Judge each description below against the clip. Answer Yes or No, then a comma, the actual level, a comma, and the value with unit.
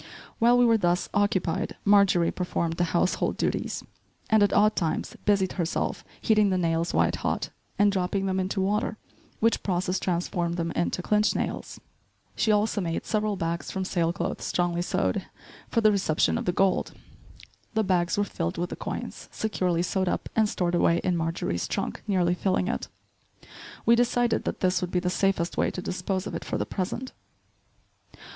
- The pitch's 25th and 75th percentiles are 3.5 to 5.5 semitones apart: No, average, 2.9 semitones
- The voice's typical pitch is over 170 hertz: Yes, medium, 185 Hz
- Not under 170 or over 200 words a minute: Yes, average, 180 wpm